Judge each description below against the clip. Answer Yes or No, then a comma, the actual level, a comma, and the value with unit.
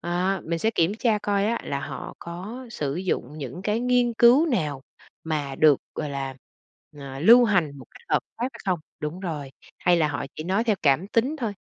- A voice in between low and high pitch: Yes, medium, 180 Hz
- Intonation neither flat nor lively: No, wide, 6.9 semitones